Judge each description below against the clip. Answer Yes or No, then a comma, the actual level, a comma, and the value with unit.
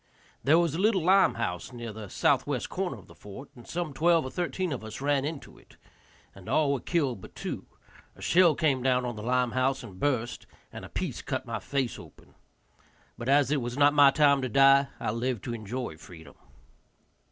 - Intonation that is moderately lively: Yes, average, 3.8 semitones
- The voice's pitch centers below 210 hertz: Yes, low, 135 Hz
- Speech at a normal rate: No, fast, 210 wpm